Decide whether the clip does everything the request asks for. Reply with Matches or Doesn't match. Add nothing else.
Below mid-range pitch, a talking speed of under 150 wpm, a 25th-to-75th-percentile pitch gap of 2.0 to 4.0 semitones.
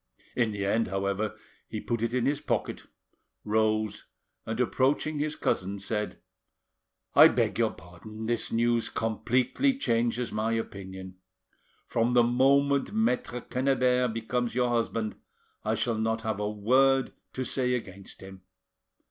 Matches